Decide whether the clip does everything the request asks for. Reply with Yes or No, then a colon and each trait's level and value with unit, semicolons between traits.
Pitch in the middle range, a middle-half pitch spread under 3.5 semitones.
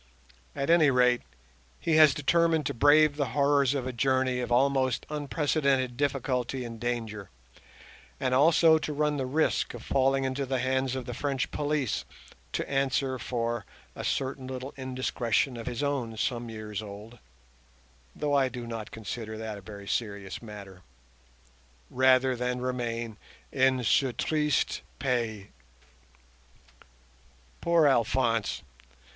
No: low, 130 Hz; average, 3.0 semitones